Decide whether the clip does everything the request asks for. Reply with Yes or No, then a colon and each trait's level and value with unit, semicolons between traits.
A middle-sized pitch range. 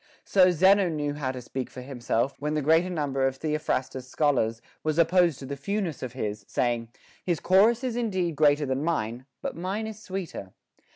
No: wide, 5.7 semitones